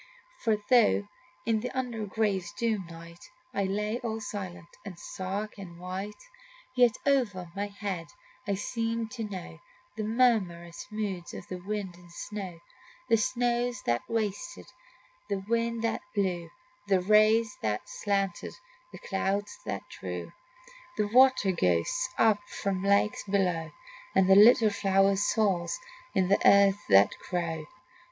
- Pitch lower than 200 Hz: No, high, 205 Hz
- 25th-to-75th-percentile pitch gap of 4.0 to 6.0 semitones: No, average, 3.2 semitones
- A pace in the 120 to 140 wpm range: Yes, slow, 135 wpm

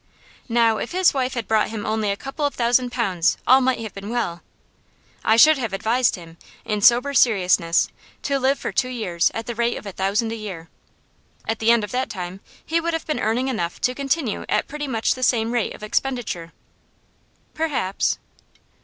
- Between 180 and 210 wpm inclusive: Yes, average, 195 wpm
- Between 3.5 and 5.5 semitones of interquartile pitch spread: Yes, average, 4.0 semitones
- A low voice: No, high, 230 Hz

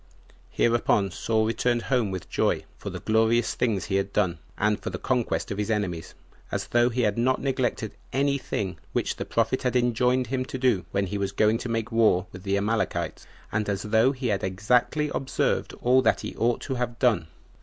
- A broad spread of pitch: No, average, 3.7 semitones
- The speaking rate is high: Yes, fast, 210 wpm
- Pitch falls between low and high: No, low, 115 Hz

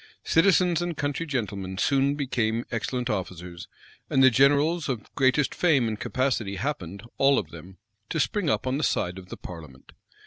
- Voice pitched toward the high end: No, low, 130 Hz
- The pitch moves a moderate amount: No, wide, 6.6 semitones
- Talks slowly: No, average, 170 wpm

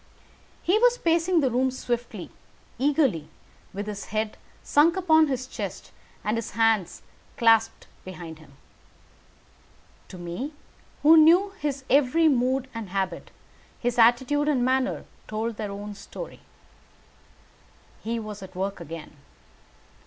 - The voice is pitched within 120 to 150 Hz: No, high, 240 Hz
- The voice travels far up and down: Yes, wide, 6.2 semitones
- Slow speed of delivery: Yes, slow, 125 wpm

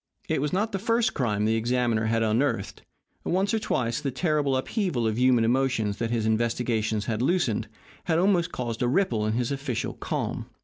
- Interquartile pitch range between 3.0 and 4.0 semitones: No, average, 5.3 semitones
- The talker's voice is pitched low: Yes, low, 125 Hz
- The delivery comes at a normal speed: Yes, average, 185 wpm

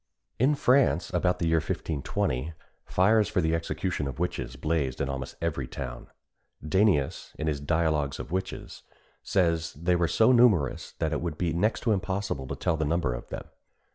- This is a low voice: Yes, very low, 85 Hz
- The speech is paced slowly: No, average, 175 wpm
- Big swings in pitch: No, average, 4.3 semitones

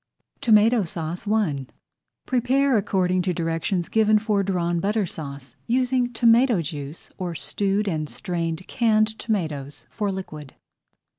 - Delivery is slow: Yes, slow, 125 wpm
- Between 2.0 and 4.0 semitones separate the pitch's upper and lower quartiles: No, average, 5.0 semitones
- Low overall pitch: No, high, 195 Hz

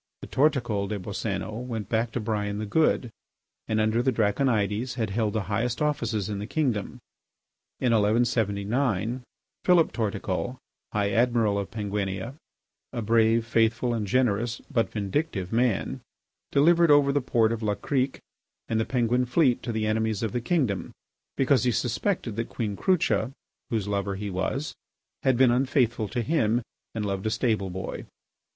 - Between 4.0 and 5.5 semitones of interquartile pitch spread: No, average, 3.3 semitones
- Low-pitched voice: Yes, low, 115 Hz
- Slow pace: No, average, 160 wpm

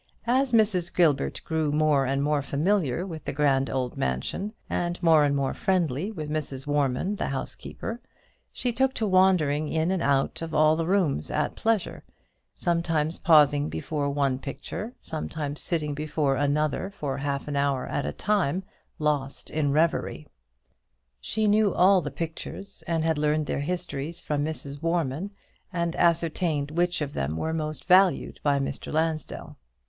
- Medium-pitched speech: Yes, medium, 155 Hz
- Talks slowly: No, average, 160 wpm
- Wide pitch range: No, average, 3.6 semitones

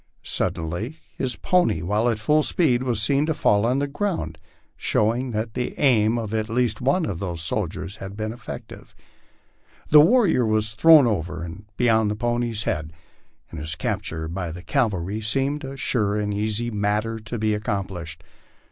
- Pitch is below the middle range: Yes, low, 110 Hz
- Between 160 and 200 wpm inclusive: Yes, average, 170 wpm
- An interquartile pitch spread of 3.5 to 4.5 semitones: Yes, average, 3.9 semitones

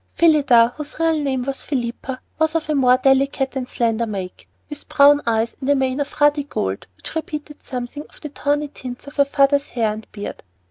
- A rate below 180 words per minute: No, fast, 205 wpm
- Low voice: No, very high, 275 Hz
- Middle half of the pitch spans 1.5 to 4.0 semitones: Yes, average, 3.1 semitones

